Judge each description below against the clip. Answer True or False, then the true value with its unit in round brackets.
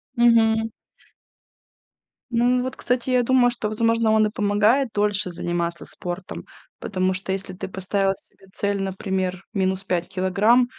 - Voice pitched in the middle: False (205 Hz)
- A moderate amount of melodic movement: True (3.5 semitones)